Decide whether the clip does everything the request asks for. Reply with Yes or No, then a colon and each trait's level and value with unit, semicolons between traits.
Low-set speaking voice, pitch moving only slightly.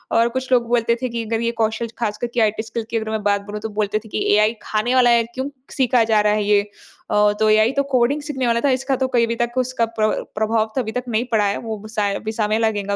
No: high, 225 Hz; narrow, 2.1 semitones